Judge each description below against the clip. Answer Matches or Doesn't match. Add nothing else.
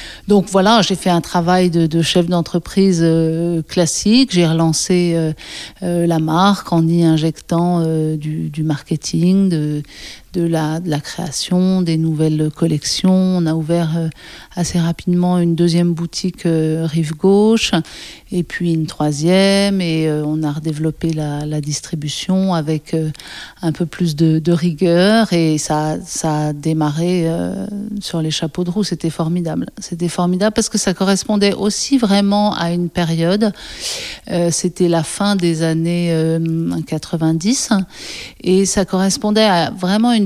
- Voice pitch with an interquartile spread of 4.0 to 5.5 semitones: Doesn't match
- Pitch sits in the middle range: Matches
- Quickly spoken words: Doesn't match